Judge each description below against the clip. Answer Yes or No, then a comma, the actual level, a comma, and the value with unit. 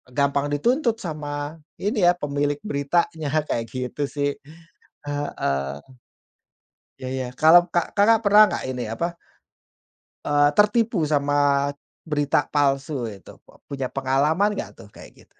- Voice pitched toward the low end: No, medium, 145 Hz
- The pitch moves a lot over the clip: No, average, 3.8 semitones